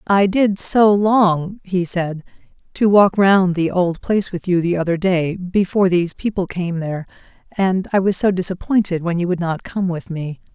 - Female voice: Yes, female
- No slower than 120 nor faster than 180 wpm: No, average, 195 wpm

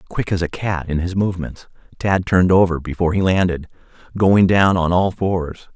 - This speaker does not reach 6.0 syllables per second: Yes, 5.3 syllables/s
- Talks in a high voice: No, very low, 90 Hz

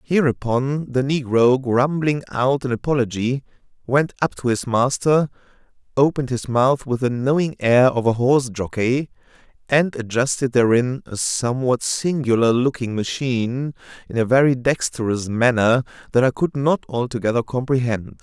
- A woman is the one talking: No, male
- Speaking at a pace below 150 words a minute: Yes, average, 140 wpm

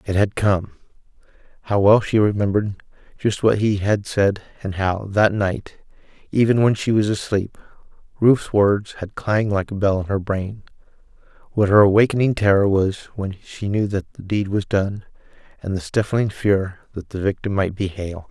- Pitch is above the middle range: No, low, 100 Hz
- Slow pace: No, average, 170 wpm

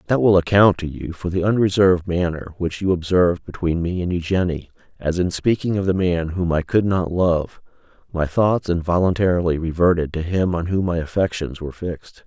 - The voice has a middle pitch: No, very low, 90 Hz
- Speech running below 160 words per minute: No, average, 190 wpm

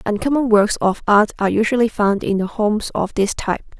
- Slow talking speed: No, fast, 205 wpm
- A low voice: No, high, 215 Hz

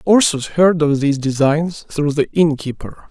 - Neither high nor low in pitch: Yes, medium, 155 Hz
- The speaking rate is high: No, average, 175 wpm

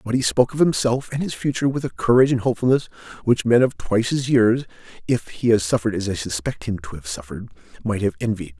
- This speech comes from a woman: No, male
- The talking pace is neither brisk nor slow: No, fast, 230 wpm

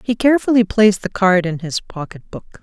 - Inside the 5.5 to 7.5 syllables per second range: Yes, 5.8 syllables/s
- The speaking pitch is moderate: No, high, 200 Hz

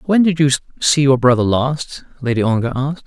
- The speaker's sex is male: Yes, male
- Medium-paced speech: Yes, average, 195 wpm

